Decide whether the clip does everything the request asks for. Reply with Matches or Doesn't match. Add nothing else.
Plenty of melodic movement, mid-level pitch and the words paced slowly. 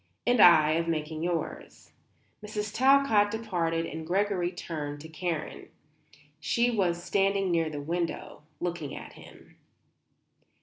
Doesn't match